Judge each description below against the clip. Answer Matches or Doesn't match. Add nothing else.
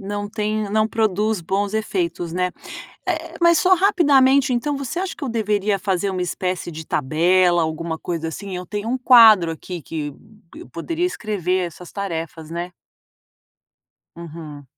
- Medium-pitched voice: Doesn't match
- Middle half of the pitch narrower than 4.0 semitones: Doesn't match